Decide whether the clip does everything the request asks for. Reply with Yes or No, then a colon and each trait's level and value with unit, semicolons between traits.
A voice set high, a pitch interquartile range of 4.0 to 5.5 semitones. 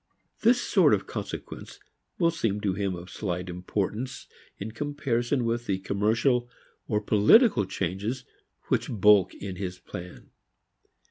No: low, 105 Hz; average, 4.3 semitones